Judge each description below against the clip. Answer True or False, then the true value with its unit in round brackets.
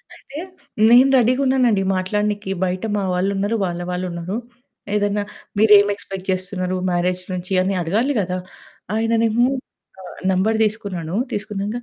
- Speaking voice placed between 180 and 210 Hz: True (200 Hz)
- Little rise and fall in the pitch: False (3.1 semitones)